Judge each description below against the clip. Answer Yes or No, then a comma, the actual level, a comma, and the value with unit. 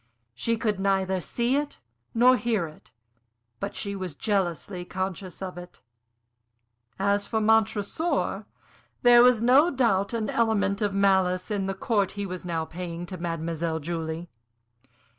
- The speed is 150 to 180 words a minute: No, average, 140 wpm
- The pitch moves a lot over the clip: No, average, 3.8 semitones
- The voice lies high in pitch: Yes, high, 195 Hz